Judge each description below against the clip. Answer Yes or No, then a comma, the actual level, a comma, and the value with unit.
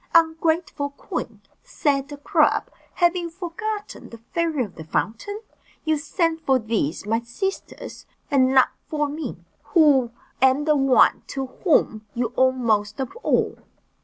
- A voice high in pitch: Yes, very high, 285 Hz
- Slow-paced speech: No, average, 145 wpm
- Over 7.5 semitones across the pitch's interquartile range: No, average, 5.3 semitones